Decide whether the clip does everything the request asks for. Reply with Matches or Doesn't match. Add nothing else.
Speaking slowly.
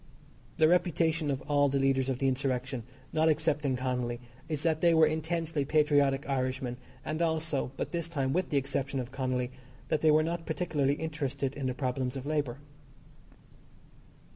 Doesn't match